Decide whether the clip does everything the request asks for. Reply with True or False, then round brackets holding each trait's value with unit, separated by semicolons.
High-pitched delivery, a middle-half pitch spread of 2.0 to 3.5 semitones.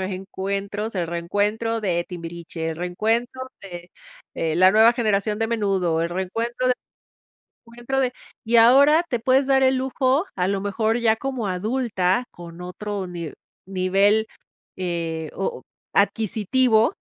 False (205 Hz; 4.8 semitones)